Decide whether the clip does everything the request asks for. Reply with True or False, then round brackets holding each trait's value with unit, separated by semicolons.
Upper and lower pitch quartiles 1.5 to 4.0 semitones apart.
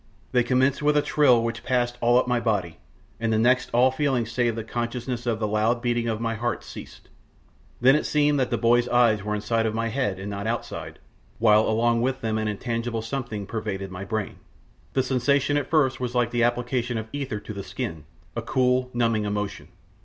True (2.5 semitones)